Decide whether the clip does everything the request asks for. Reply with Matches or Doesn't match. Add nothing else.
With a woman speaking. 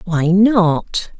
Matches